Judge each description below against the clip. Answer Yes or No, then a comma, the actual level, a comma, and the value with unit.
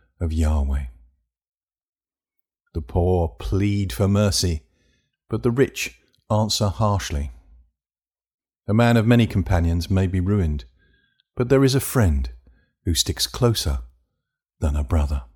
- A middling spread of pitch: No, wide, 6.0 semitones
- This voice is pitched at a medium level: No, very low, 85 Hz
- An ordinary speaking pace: No, slow, 120 wpm